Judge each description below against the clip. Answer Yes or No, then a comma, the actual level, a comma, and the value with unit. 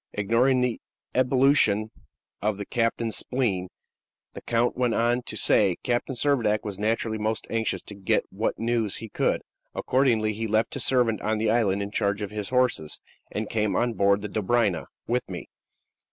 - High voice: No, low, 110 Hz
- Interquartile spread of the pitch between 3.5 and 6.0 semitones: No, average, 2.7 semitones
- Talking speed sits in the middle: Yes, average, 170 wpm